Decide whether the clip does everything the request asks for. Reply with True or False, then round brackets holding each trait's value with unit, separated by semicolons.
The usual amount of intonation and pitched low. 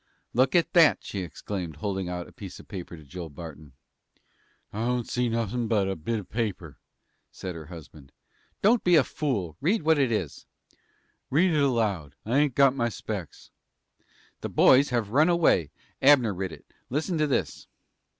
False (7.7 semitones; 110 Hz)